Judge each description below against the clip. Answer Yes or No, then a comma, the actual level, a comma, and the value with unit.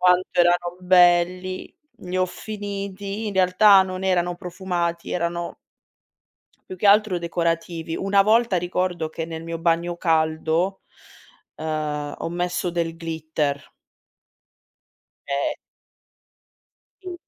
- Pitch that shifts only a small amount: Yes, narrow, 2.1 semitones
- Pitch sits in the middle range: Yes, medium, 175 Hz